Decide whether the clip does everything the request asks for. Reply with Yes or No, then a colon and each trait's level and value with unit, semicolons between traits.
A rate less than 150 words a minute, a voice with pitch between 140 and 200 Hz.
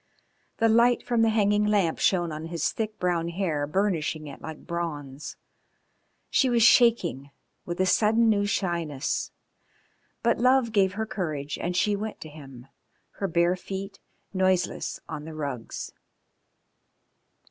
Yes: average, 140 wpm; medium, 185 Hz